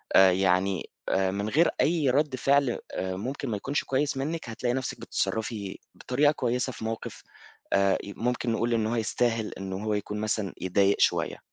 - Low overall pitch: Yes, low, 115 Hz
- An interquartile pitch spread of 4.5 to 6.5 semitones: Yes, average, 4.8 semitones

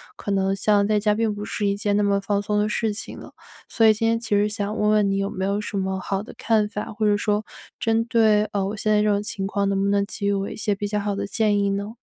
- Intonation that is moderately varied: No, narrow, 1.1 semitones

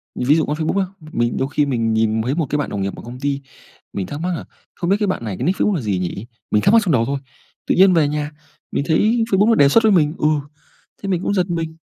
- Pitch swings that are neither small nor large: No, wide, 7.5 semitones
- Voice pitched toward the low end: No, medium, 150 Hz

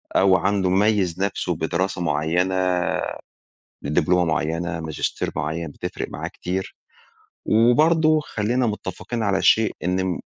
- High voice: No, very low, 95 Hz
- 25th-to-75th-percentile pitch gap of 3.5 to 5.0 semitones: Yes, average, 4.0 semitones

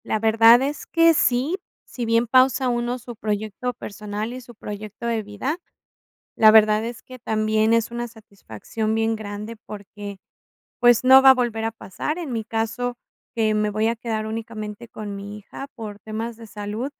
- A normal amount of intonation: No, narrow, 2.2 semitones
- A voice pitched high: Yes, high, 225 Hz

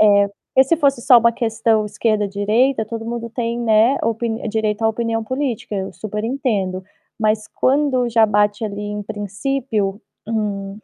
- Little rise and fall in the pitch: Yes, narrow, 2.3 semitones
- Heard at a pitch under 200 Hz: No, high, 220 Hz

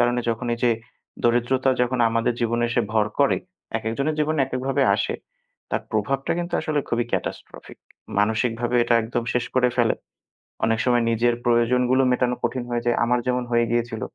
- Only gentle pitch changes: Yes, narrow, 1.5 semitones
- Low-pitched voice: Yes, low, 120 Hz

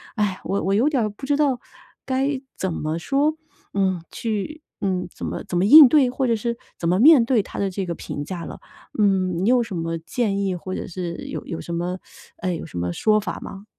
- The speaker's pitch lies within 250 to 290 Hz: No, high, 200 Hz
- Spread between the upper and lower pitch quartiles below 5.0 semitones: No, wide, 5.6 semitones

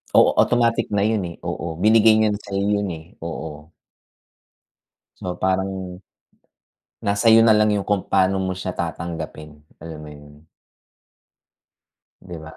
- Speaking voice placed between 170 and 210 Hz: No, very low, 95 Hz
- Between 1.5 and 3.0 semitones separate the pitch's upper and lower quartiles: No, average, 4.1 semitones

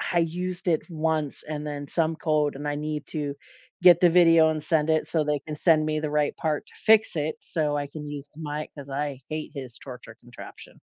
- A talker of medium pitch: Yes, medium, 155 Hz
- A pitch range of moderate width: No, narrow, 1.7 semitones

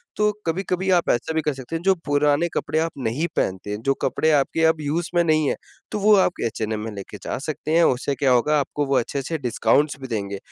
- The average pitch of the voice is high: No, medium, 145 Hz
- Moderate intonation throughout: Yes, average, 4.7 semitones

